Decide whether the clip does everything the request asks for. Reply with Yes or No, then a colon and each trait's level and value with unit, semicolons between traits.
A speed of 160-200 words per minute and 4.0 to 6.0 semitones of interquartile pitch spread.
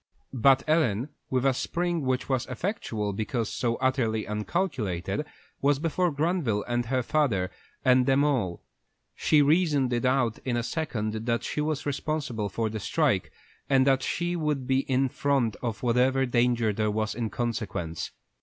Yes: average, 165 wpm; average, 4.3 semitones